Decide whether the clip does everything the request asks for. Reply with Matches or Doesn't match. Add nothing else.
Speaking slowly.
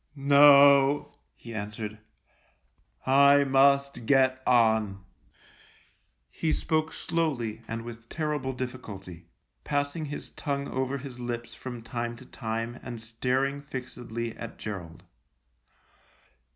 Matches